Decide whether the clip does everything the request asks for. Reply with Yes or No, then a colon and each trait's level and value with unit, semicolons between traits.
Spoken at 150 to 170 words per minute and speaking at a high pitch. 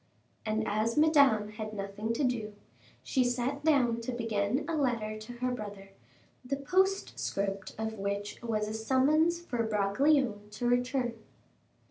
No: average, 140 wpm; high, 230 Hz